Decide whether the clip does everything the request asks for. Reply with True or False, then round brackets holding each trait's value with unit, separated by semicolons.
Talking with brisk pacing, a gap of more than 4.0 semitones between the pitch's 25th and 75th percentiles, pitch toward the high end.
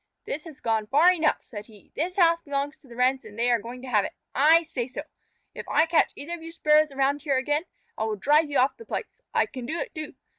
True (260 wpm; 4.4 semitones; 285 Hz)